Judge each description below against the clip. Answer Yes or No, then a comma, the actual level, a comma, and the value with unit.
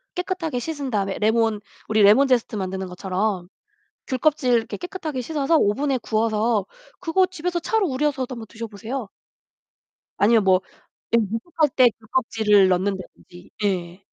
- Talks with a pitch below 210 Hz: No, high, 230 Hz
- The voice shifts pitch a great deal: Yes, wide, 5.9 semitones